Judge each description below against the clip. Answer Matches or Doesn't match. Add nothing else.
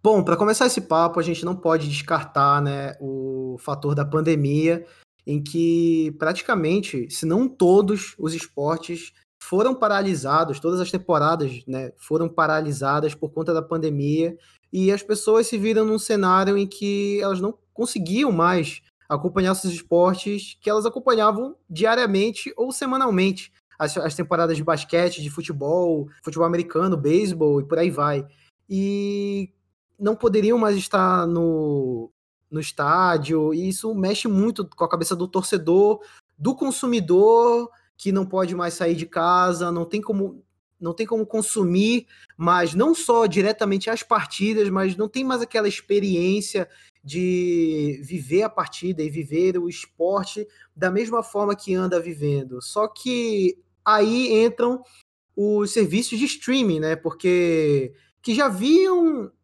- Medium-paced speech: Matches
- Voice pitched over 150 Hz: Matches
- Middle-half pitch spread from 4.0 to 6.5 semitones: Matches